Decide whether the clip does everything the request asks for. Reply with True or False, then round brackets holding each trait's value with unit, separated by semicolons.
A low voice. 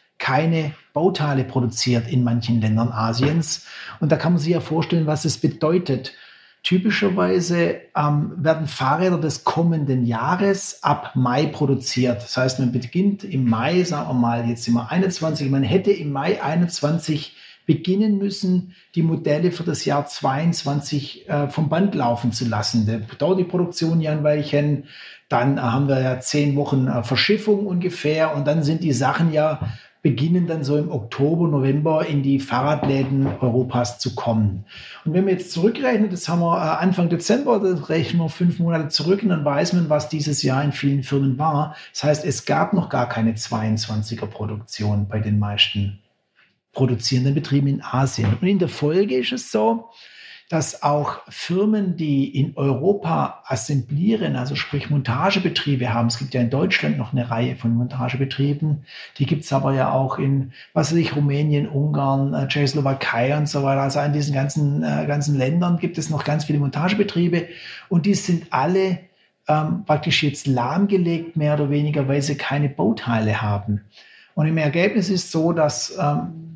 False (145 Hz)